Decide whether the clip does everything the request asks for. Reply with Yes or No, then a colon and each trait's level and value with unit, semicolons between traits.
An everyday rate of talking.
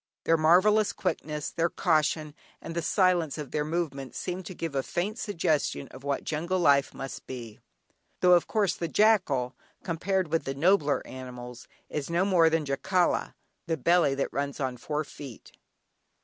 Yes: average, 165 wpm